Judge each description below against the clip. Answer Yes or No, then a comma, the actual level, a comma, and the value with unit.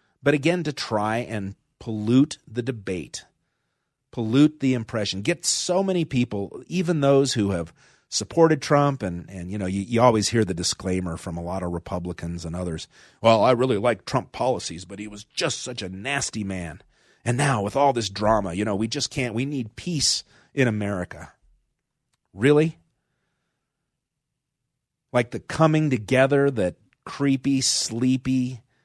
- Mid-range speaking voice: No, low, 120 Hz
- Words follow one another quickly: No, average, 160 wpm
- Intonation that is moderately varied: No, wide, 6.1 semitones